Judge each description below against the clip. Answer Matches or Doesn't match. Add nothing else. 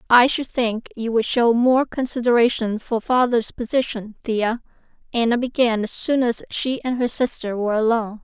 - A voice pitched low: Doesn't match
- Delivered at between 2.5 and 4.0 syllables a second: Doesn't match